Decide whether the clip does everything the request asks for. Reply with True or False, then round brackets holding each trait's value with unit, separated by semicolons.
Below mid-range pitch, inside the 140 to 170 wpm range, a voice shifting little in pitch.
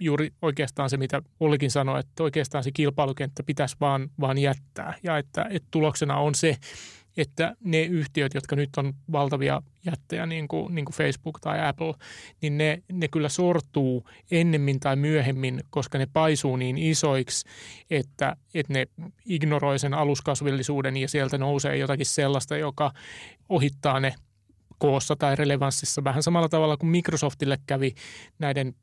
False (145 Hz; 150 wpm; 2.1 semitones)